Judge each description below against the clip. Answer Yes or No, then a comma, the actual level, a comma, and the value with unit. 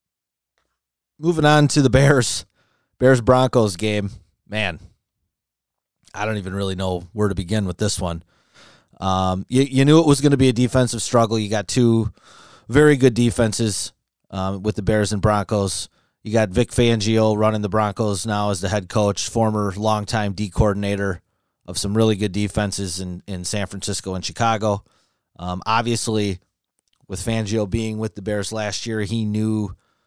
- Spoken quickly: No, average, 165 wpm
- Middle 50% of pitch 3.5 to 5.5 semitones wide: No, narrow, 2.5 semitones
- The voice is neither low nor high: No, low, 105 Hz